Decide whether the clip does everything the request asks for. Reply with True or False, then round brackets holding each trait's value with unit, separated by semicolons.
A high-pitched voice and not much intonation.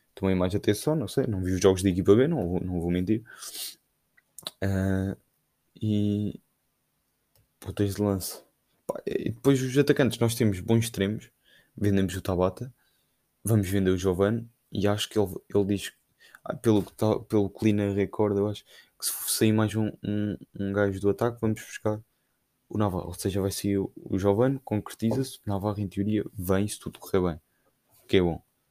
False (100 Hz; 2.3 semitones)